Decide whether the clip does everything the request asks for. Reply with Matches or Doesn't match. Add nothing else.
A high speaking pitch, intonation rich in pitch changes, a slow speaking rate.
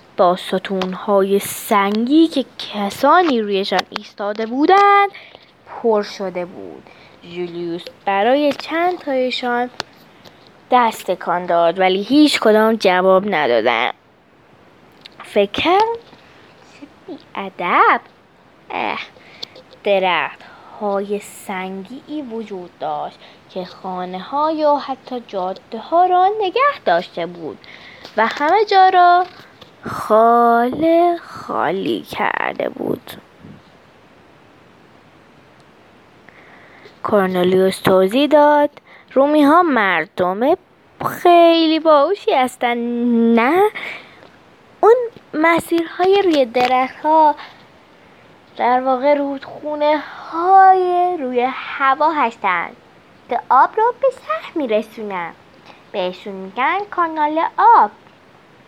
Matches